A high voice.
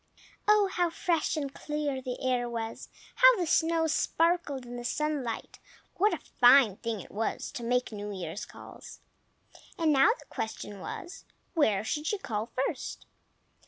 Yes: very high, 270 Hz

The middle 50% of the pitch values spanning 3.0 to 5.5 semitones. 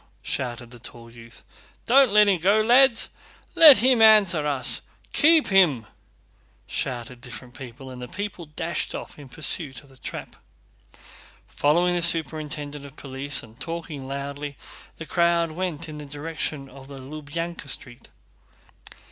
Yes: average, 4.6 semitones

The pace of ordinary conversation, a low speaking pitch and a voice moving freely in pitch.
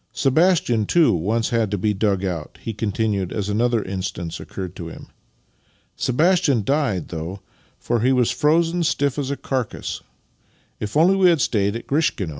Yes: average, 170 wpm; low, 115 Hz; wide, 6.6 semitones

